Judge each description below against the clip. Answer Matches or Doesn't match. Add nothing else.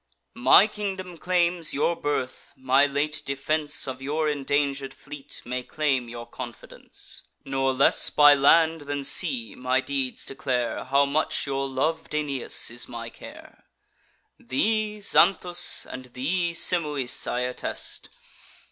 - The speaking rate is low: Matches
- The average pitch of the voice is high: Doesn't match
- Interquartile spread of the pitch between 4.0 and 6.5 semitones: Doesn't match